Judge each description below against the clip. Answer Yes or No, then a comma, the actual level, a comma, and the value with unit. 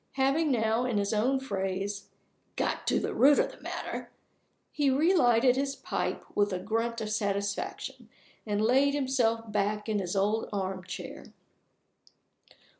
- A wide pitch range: No, average, 4.6 semitones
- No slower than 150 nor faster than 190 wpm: No, average, 140 wpm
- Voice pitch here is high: Yes, high, 220 Hz